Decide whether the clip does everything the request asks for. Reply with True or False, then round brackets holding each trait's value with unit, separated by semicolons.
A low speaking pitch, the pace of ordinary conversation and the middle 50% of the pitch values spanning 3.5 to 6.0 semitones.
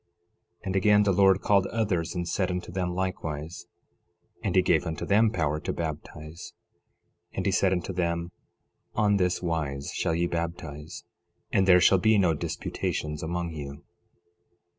False (85 Hz; 160 wpm; 2.8 semitones)